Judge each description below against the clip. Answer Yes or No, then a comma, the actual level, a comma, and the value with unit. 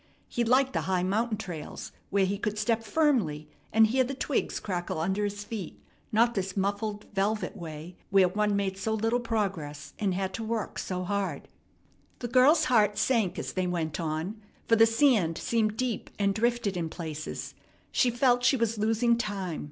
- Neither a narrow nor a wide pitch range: Yes, average, 3.8 semitones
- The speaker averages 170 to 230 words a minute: Yes, average, 180 wpm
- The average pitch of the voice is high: Yes, high, 210 Hz